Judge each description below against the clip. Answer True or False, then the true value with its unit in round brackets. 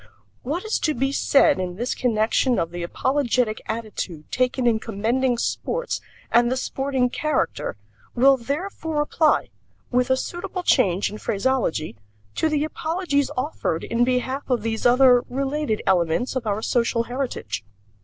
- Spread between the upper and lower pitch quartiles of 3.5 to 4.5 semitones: True (3.9 semitones)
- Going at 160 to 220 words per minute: False (145 wpm)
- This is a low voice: False (250 Hz)